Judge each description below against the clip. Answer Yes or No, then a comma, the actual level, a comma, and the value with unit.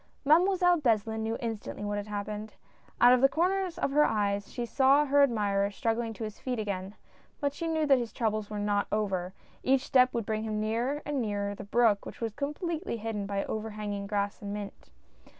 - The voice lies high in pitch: Yes, high, 220 Hz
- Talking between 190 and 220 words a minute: Yes, fast, 205 wpm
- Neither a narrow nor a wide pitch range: Yes, average, 4.8 semitones